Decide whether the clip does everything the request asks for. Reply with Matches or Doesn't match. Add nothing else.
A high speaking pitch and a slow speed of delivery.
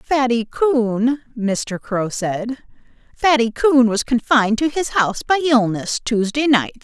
Matches